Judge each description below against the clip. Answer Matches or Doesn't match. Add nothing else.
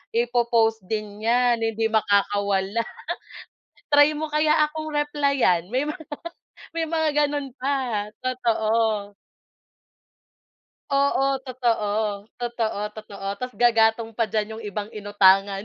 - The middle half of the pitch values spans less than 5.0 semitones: Matches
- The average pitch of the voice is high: Matches